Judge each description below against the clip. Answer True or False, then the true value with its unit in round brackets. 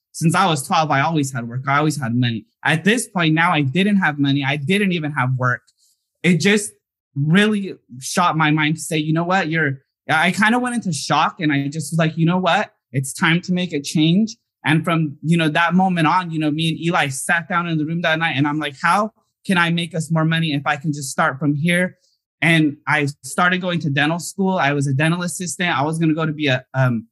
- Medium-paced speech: False (250 wpm)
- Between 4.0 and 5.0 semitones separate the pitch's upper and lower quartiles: False (3.3 semitones)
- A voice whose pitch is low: False (160 Hz)